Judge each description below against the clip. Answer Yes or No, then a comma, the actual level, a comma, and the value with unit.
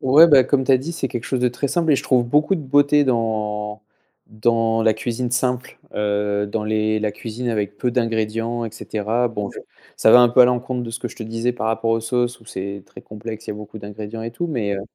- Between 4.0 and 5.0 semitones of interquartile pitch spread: No, average, 2.7 semitones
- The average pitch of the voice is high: No, low, 115 Hz